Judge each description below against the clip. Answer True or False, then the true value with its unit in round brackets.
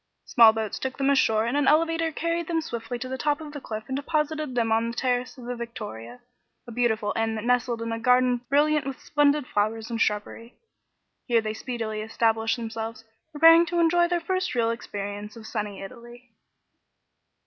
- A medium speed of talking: True (190 wpm)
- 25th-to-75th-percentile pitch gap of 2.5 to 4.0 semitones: False (4.5 semitones)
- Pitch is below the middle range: False (240 Hz)